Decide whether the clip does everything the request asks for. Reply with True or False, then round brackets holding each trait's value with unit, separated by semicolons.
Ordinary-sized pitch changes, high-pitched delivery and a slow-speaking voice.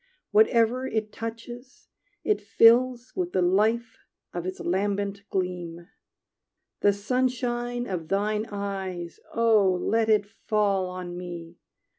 True (4.1 semitones; 205 Hz; 115 wpm)